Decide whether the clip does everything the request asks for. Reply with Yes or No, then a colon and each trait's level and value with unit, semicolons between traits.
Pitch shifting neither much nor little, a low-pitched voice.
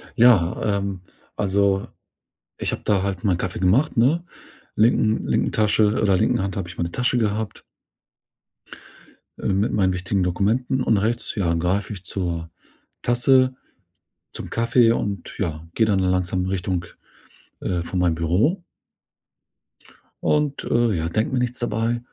Yes: average, 4.3 semitones; low, 100 Hz